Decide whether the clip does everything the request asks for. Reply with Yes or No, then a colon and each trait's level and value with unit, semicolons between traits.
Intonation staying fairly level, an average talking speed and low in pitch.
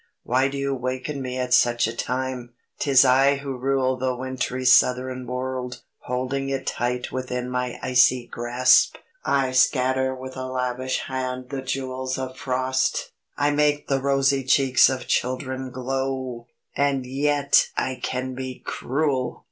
Yes: narrow, 1.0 semitones; average, 150 wpm; low, 130 Hz